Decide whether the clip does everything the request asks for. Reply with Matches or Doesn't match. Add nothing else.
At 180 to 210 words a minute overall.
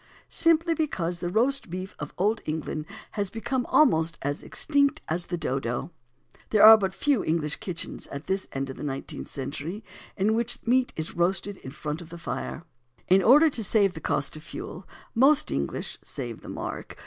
Matches